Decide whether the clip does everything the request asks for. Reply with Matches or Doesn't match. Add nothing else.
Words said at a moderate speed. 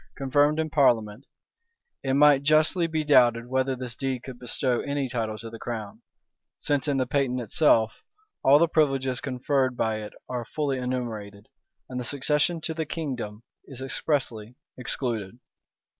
Matches